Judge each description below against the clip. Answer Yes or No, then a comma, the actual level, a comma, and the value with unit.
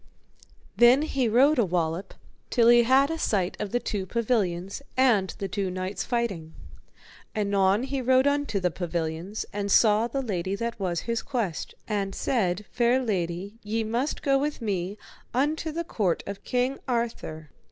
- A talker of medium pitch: No, high, 215 Hz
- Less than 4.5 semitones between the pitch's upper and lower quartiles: No, average, 4.8 semitones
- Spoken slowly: No, average, 165 wpm